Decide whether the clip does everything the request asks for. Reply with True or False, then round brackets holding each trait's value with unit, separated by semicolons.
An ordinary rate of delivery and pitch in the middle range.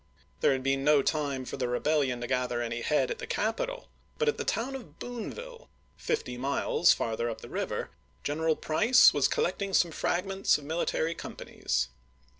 True (175 wpm; 155 Hz)